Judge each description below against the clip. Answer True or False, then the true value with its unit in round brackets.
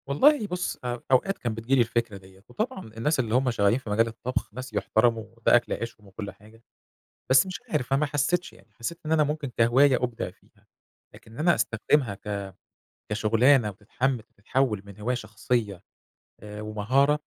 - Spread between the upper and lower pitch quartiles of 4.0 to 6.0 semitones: True (4.3 semitones)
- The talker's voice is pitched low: True (120 Hz)